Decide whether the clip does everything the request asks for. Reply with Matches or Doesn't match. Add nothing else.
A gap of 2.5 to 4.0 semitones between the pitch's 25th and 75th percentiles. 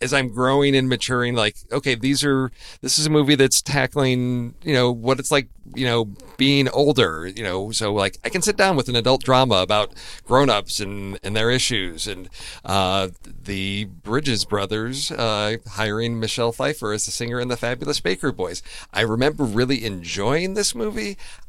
Doesn't match